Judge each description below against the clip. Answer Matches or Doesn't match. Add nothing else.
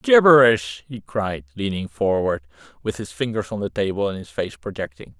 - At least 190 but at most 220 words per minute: Doesn't match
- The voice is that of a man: Matches